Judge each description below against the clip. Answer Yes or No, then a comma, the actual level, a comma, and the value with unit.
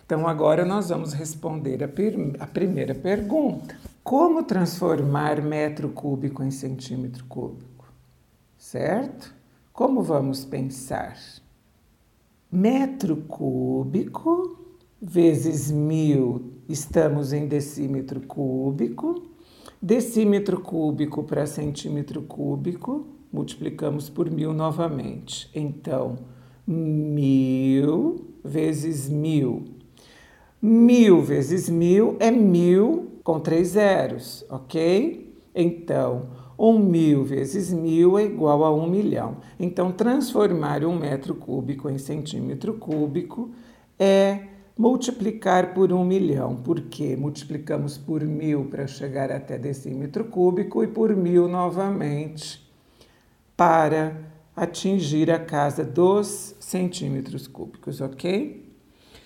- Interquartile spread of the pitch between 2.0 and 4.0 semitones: No, average, 5.3 semitones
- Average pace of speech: No, slow, 95 wpm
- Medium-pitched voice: Yes, medium, 155 Hz